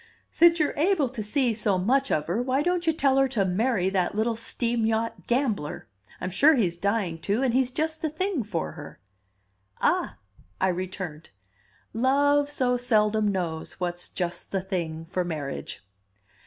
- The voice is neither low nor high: No, high, 225 Hz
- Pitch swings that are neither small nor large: No, wide, 6.7 semitones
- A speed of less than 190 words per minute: Yes, average, 170 wpm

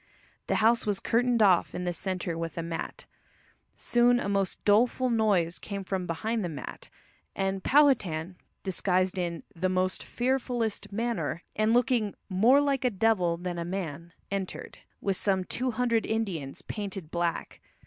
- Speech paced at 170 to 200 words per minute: No, average, 155 wpm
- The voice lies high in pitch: Yes, high, 195 Hz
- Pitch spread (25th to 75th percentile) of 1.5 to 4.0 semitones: No, average, 4.5 semitones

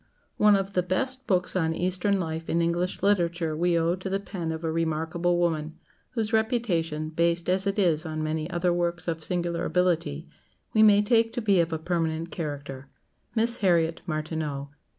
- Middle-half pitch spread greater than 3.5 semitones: No, average, 2.9 semitones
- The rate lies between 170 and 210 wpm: Yes, average, 180 wpm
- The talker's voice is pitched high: No, medium, 170 Hz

